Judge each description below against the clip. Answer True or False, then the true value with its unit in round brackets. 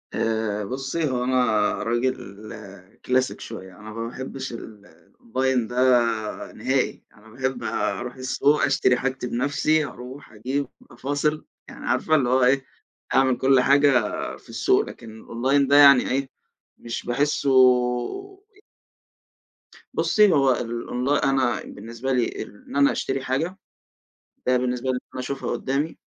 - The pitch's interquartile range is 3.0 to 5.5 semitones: False (2.4 semitones)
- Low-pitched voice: True (130 Hz)